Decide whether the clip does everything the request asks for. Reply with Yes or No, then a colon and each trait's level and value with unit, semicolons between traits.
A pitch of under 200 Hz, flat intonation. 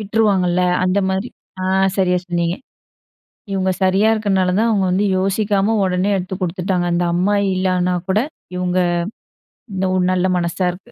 Yes: medium, 185 Hz; narrow, 1.5 semitones